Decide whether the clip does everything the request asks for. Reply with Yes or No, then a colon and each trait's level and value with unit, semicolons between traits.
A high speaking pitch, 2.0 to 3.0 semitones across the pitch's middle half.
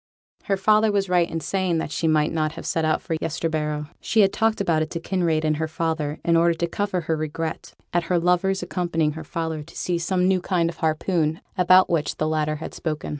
No: medium, 165 Hz; narrow, 2.5 semitones